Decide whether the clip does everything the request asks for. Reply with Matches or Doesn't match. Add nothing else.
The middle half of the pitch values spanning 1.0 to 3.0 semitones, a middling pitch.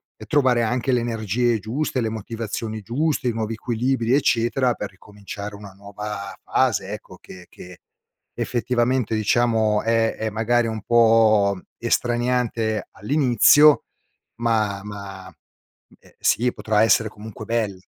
Doesn't match